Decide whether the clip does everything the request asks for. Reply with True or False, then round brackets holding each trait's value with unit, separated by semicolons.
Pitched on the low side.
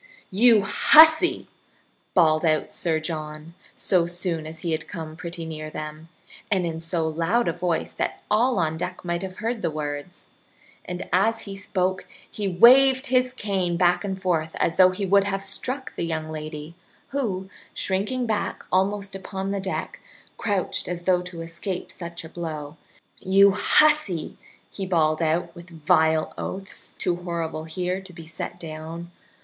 False (180 Hz)